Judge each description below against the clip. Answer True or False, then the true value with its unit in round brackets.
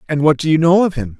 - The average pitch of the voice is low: False (160 Hz)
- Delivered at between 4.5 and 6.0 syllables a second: False (6.9 syllables/s)